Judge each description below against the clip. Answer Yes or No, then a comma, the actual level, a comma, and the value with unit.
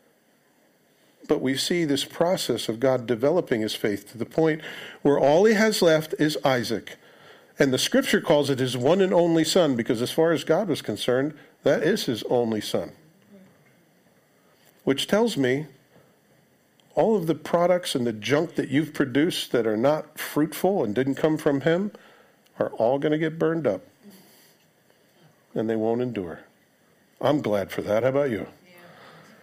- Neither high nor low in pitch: Yes, medium, 155 Hz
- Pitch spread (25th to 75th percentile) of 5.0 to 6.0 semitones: Yes, average, 5.3 semitones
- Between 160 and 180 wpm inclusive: Yes, average, 165 wpm